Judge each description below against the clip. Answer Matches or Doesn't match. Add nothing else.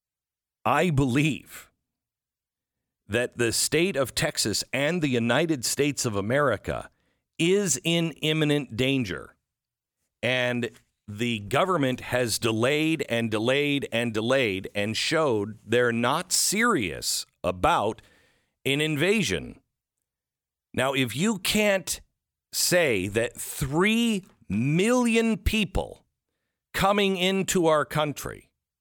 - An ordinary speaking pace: Doesn't match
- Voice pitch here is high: Doesn't match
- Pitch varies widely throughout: Matches